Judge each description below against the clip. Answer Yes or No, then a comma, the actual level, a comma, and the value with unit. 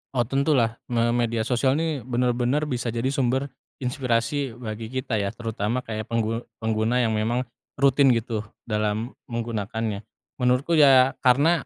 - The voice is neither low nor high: No, low, 120 Hz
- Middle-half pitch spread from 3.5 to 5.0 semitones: No, average, 2.7 semitones